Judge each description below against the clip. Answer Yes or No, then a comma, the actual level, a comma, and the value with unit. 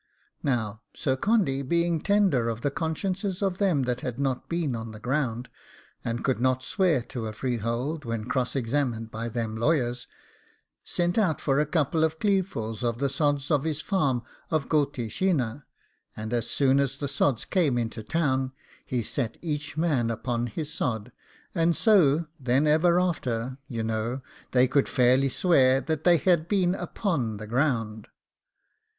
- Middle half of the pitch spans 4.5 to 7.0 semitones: Yes, average, 5.1 semitones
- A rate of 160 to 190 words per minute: Yes, average, 165 wpm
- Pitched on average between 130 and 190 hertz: Yes, low, 135 Hz